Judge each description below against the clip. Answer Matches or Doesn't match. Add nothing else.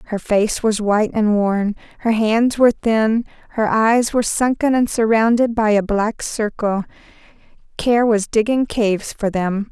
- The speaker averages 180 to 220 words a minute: Doesn't match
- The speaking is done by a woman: Matches